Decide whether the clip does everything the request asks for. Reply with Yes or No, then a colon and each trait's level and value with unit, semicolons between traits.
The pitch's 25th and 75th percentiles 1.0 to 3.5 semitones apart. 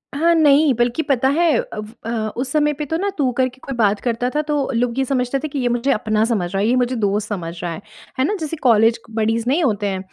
No: average, 4.6 semitones